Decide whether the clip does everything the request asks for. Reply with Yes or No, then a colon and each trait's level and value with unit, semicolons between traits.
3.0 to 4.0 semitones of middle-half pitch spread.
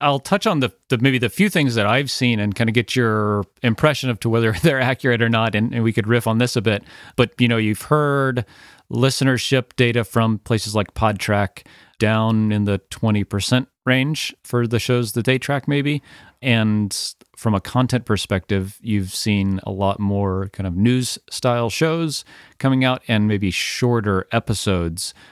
Yes: average, 3.6 semitones